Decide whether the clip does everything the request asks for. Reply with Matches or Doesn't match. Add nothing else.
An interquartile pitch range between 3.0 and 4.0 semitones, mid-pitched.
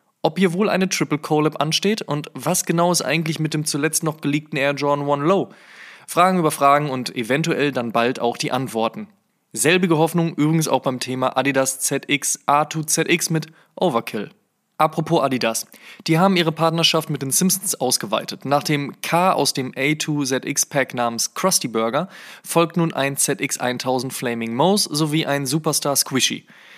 Matches